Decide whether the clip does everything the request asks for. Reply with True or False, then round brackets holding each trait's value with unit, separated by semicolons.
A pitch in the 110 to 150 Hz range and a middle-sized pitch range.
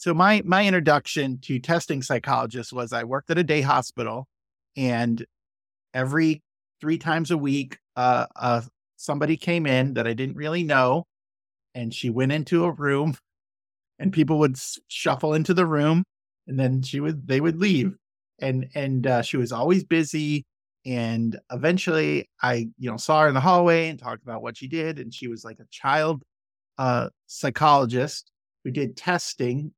True (135 Hz; 4.5 semitones)